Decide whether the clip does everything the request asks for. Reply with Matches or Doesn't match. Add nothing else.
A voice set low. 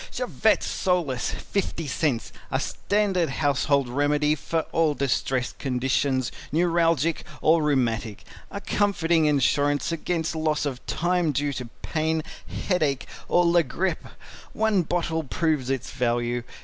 Doesn't match